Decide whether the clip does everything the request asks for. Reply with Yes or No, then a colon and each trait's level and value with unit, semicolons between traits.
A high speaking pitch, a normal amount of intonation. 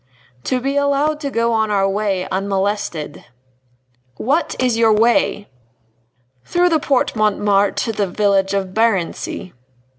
Yes: high, 215 Hz; average, 4.5 semitones